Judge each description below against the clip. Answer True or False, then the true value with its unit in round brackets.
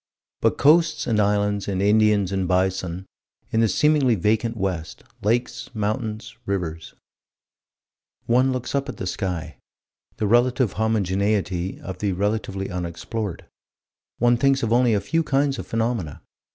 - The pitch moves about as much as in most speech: True (4.1 semitones)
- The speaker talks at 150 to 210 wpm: False (140 wpm)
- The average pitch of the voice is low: True (105 Hz)